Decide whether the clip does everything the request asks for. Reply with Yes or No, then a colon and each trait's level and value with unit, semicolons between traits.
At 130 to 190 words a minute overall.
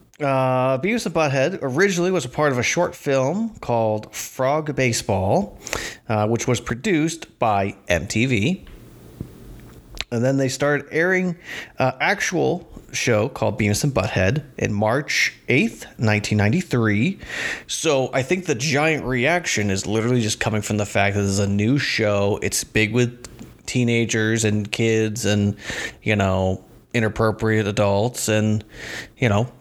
Yes: average, 140 wpm